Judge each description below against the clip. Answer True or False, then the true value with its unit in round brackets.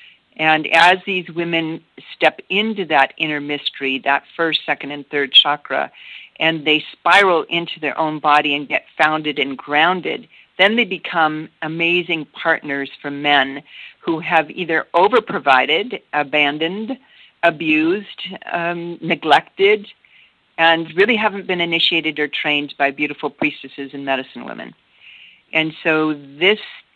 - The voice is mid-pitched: True (155 Hz)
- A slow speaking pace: True (130 wpm)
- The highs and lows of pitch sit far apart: False (2.7 semitones)